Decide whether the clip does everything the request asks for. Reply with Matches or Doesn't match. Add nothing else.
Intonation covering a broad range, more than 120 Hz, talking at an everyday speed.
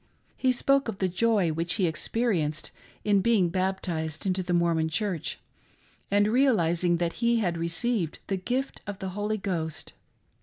Doesn't match